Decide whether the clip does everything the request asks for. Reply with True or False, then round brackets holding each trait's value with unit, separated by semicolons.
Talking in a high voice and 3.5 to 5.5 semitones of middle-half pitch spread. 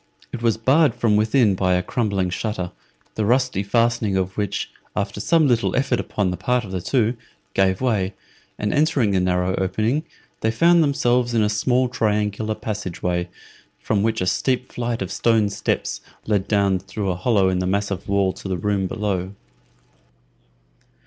False (105 Hz; 4.0 semitones)